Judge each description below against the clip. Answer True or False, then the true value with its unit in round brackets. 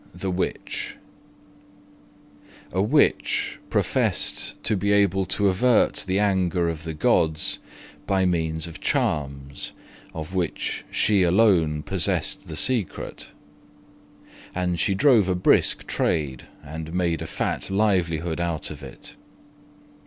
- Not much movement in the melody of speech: False (3.3 semitones)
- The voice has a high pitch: False (90 Hz)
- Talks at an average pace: False (120 wpm)